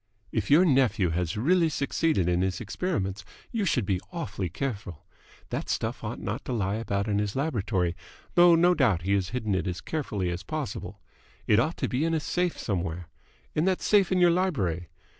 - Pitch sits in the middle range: No, low, 110 Hz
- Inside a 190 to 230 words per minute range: Yes, average, 195 wpm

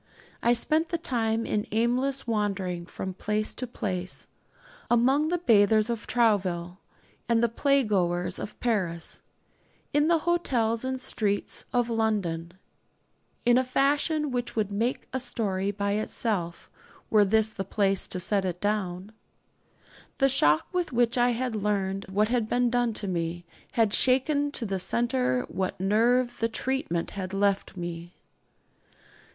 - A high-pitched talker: Yes, high, 220 Hz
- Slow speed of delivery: No, average, 145 wpm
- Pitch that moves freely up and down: No, average, 4.3 semitones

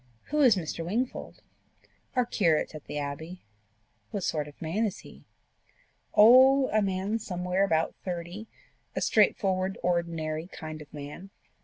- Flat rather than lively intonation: No, average, 4.7 semitones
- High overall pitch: No, medium, 180 Hz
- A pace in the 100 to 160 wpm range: Yes, average, 140 wpm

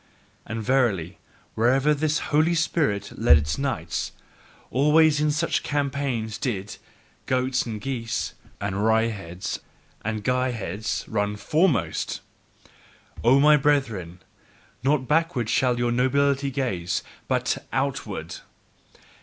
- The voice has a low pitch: Yes, low, 125 Hz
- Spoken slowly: Yes, slow, 105 wpm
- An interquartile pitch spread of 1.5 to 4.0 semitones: No, average, 5.1 semitones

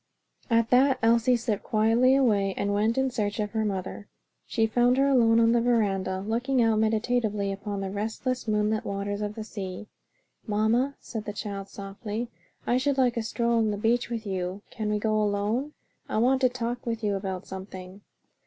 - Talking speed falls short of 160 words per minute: No, average, 190 wpm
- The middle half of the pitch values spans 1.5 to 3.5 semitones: Yes, average, 2.9 semitones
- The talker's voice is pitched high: Yes, high, 220 Hz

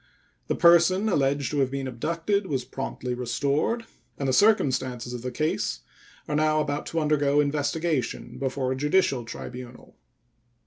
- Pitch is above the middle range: No, medium, 145 Hz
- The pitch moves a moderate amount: Yes, average, 3.5 semitones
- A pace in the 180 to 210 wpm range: No, average, 145 wpm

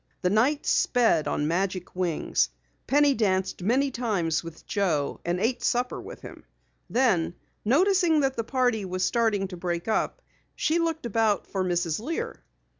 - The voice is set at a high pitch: Yes, high, 215 Hz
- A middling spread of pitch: No, wide, 6.3 semitones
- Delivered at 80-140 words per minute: No, average, 155 wpm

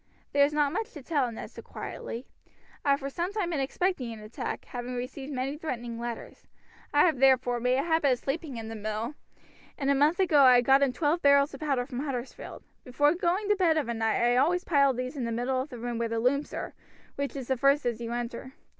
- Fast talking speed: Yes, fast, 240 wpm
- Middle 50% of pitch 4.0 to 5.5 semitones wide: No, average, 3.3 semitones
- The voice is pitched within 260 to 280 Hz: Yes, very high, 270 Hz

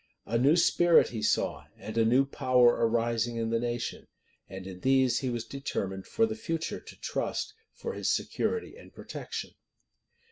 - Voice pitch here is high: No, low, 120 Hz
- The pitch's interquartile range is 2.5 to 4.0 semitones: Yes, average, 3.4 semitones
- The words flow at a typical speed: Yes, average, 170 wpm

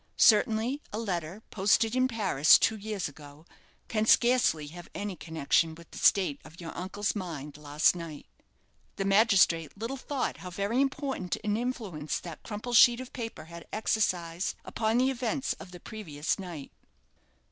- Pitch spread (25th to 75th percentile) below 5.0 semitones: No, wide, 5.4 semitones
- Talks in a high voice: Yes, high, 200 Hz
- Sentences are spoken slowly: No, average, 160 wpm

